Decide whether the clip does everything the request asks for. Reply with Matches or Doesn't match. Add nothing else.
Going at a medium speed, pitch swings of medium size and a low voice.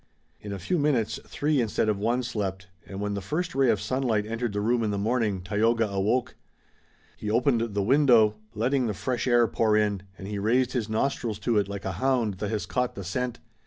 Doesn't match